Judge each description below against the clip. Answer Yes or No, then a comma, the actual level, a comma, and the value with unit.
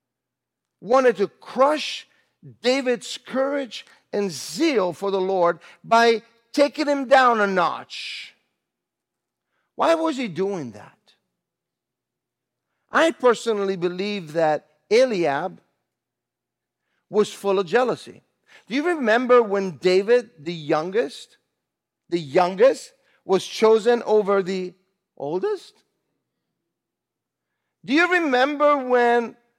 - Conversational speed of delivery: No, slow, 95 wpm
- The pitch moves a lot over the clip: Yes, wide, 5.9 semitones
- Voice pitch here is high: Yes, high, 230 Hz